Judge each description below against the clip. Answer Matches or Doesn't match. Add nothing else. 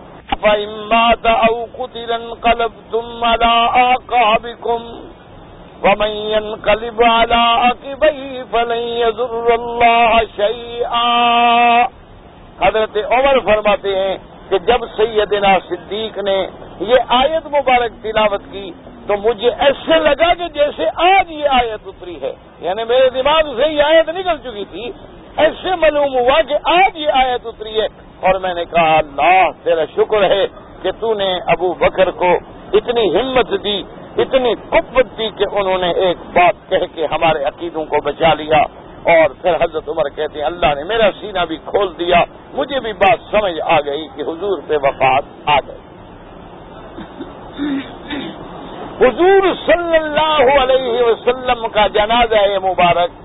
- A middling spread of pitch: Matches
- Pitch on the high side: Matches